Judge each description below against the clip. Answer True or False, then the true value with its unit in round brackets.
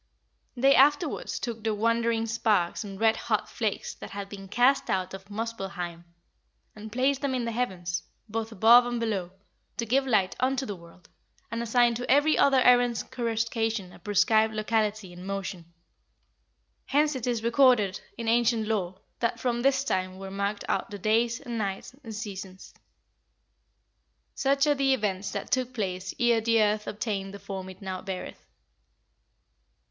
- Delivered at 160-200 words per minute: True (165 wpm)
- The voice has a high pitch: True (220 Hz)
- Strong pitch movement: False (3.8 semitones)